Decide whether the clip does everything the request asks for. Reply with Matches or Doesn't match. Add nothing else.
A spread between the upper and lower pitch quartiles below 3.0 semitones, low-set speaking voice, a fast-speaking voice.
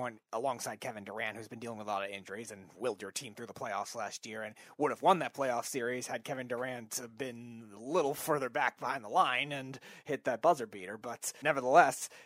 Matches